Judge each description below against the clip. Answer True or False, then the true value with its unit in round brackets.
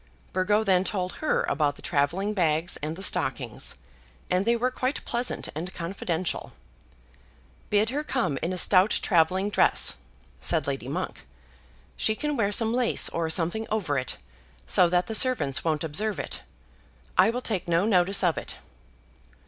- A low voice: False (185 Hz)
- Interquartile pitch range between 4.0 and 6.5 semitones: True (5.0 semitones)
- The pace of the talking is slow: False (160 wpm)